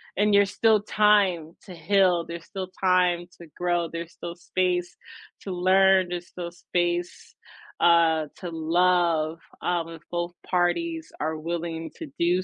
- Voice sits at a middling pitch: Yes, medium, 175 Hz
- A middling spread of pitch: No, narrow, 1.7 semitones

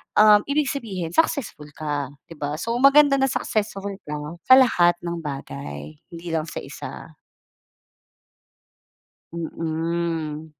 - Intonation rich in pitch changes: Yes, wide, 6.1 semitones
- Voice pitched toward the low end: No, medium, 170 Hz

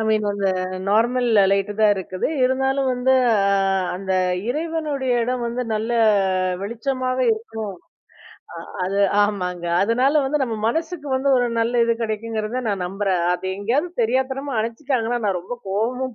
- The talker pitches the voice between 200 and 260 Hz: Yes, high, 235 Hz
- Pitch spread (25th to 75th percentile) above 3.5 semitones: Yes, average, 4.2 semitones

